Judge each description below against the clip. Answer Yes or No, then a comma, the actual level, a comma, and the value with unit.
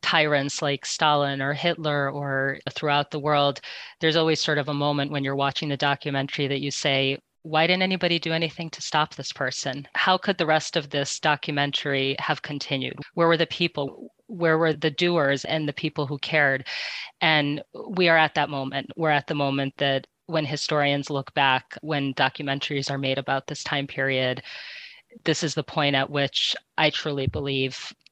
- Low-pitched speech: No, medium, 145 Hz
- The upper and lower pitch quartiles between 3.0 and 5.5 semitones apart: No, narrow, 2.4 semitones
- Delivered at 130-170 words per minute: No, average, 185 wpm